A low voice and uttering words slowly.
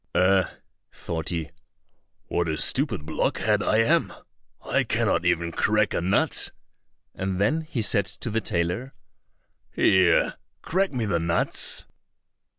Yes: very low, 95 Hz; slow, 130 wpm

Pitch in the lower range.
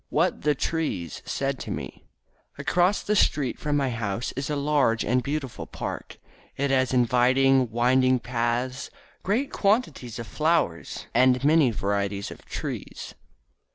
Yes: low, 130 Hz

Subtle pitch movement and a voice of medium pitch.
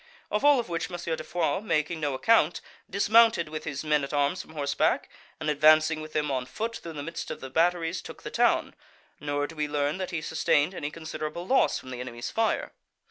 No: average, 3.3 semitones; medium, 155 Hz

